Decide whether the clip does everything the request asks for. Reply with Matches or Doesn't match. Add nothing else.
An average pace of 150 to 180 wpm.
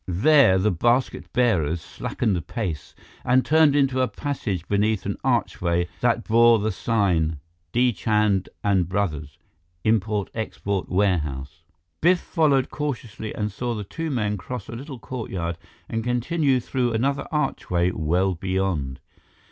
Doesn't match